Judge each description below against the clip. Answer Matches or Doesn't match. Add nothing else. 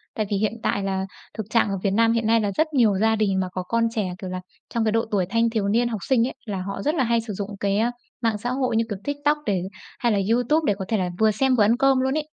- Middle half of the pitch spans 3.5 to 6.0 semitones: Doesn't match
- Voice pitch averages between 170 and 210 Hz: Doesn't match